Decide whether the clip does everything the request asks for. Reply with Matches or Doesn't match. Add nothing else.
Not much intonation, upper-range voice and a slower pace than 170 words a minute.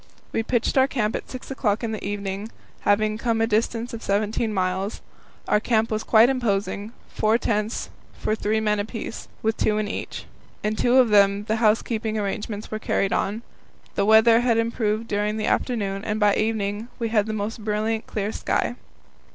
Doesn't match